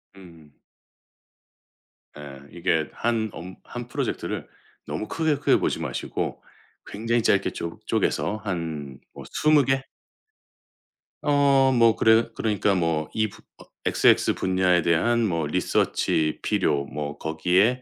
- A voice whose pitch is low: Yes, very low, 95 Hz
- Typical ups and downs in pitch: No, wide, 6.4 semitones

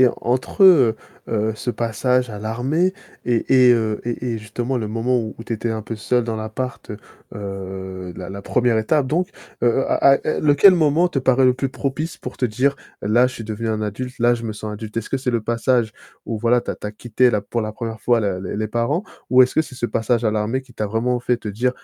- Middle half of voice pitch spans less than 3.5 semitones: Yes, average, 2.9 semitones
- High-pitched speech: No, low, 120 Hz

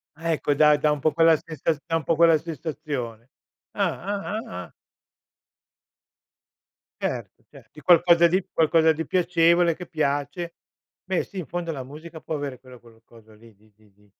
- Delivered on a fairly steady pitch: No, average, 4.4 semitones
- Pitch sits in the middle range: Yes, medium, 155 Hz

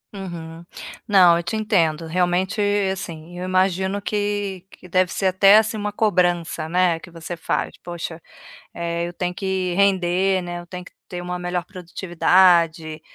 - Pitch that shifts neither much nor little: No, narrow, 1.8 semitones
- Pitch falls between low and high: Yes, medium, 180 Hz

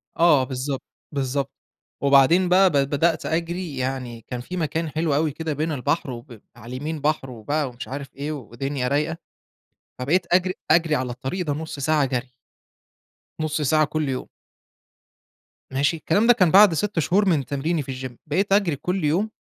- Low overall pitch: No, medium, 150 Hz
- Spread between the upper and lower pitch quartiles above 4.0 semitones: No, average, 3.7 semitones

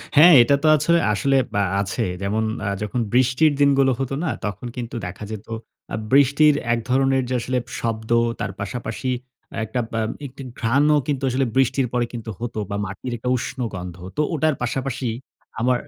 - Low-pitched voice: Yes, low, 125 Hz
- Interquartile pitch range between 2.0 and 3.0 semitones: No, average, 3.5 semitones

